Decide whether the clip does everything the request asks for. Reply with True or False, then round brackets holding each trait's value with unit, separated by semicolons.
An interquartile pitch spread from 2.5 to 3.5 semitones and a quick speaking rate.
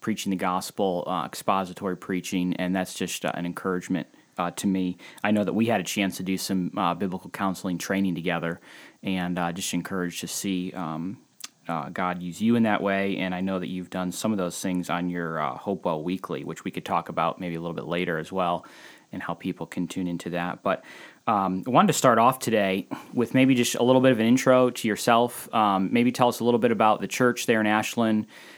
True (3.2 semitones; 230 wpm)